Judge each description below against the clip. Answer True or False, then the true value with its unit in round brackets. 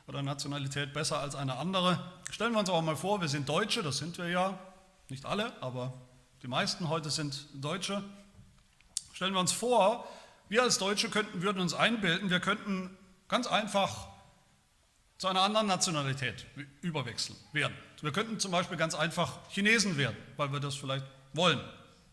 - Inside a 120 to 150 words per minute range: False (165 wpm)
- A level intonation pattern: False (5.2 semitones)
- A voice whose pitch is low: False (170 Hz)